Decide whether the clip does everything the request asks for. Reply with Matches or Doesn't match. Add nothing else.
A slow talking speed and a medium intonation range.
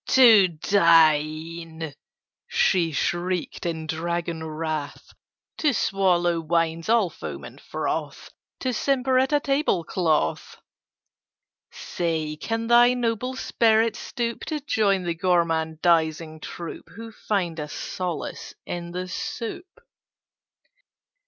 Doesn't match